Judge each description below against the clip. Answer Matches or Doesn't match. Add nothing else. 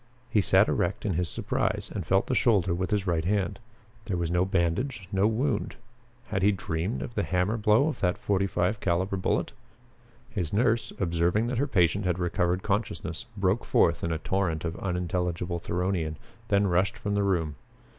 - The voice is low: Matches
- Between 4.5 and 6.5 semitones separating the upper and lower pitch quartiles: Doesn't match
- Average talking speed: Matches